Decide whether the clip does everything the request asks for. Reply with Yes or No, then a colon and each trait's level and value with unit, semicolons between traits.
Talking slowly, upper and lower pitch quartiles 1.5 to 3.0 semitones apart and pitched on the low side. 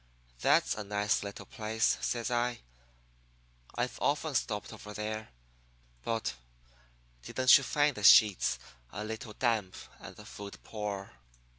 Yes: slow, 130 wpm; average, 2.7 semitones; low, 110 Hz